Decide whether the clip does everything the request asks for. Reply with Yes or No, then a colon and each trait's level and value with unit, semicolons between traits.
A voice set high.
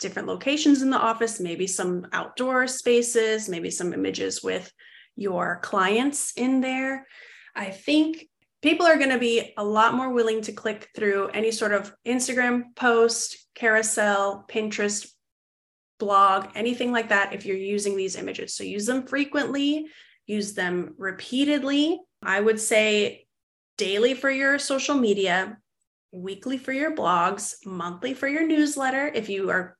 Yes: high, 225 Hz